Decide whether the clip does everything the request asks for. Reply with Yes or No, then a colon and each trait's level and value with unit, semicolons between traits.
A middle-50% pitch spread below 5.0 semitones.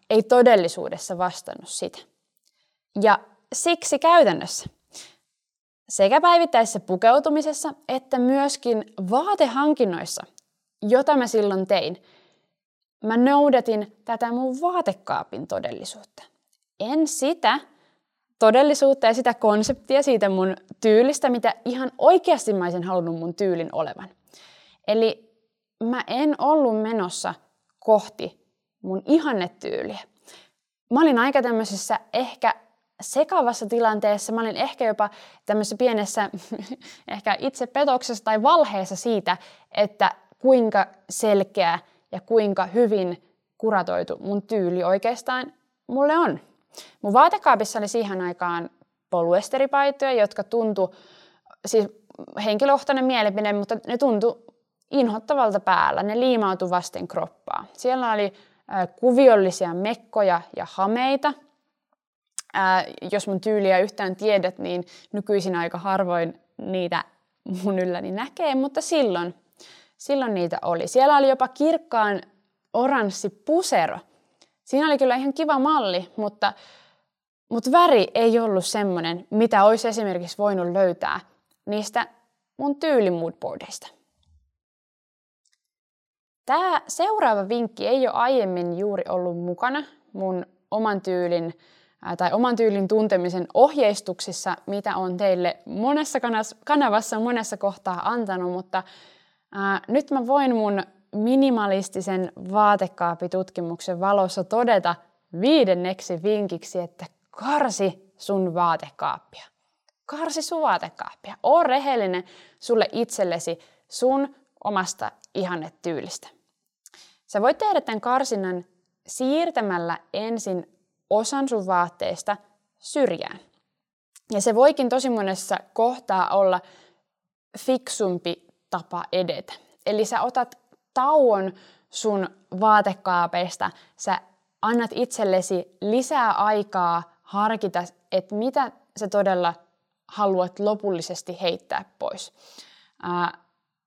No: wide, 5.5 semitones